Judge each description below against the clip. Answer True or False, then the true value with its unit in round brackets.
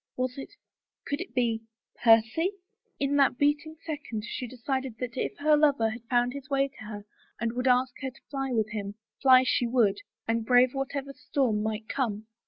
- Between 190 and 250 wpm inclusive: True (195 wpm)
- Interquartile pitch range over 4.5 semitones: False (3.4 semitones)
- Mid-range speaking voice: False (255 Hz)